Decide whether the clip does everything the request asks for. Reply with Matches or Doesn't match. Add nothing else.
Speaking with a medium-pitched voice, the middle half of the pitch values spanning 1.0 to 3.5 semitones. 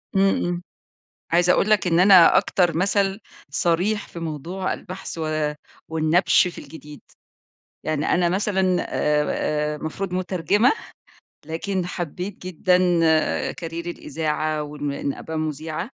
Matches